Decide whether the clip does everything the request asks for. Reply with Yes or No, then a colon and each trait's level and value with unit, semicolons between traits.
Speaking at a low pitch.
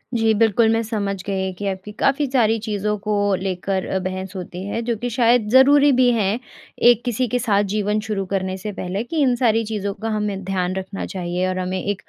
No: high, 210 Hz